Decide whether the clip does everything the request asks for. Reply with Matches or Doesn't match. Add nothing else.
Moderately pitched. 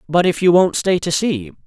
Matches